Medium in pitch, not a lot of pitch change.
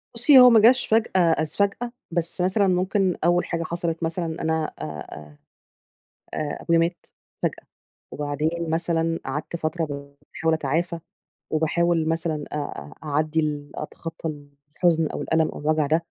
Yes: medium, 165 Hz; narrow, 2.1 semitones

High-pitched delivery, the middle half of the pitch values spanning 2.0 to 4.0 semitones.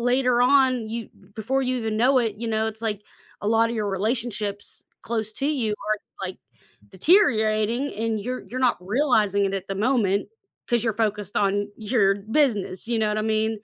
Yes: high, 220 Hz; average, 2.9 semitones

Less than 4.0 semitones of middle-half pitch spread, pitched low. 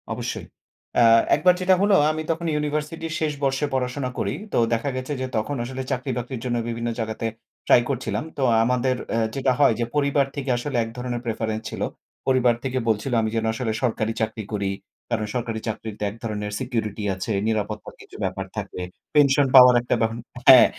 Yes: average, 3.4 semitones; low, 125 Hz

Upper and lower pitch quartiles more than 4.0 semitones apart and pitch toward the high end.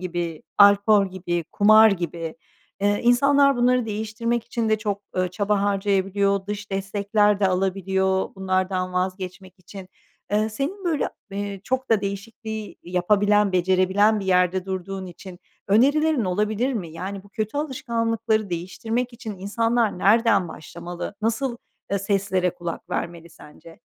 No: average, 2.9 semitones; high, 200 Hz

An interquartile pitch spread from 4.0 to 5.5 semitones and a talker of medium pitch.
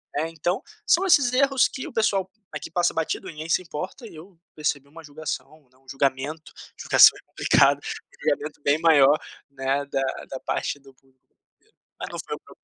Yes: average, 4.6 semitones; medium, 155 Hz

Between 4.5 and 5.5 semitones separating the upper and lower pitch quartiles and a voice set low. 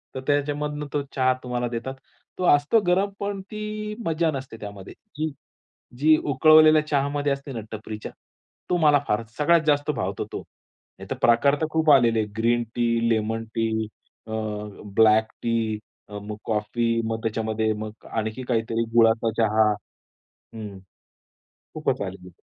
Yes: average, 5.0 semitones; low, 120 Hz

